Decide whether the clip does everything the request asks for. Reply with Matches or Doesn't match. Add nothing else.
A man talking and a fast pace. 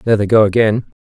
Matches